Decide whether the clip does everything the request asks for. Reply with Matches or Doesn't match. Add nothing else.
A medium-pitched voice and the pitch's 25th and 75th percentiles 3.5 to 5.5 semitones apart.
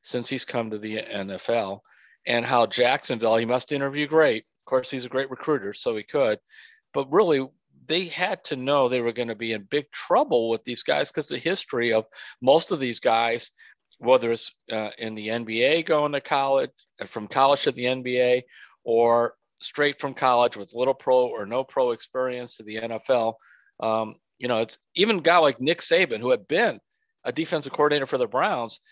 Doesn't match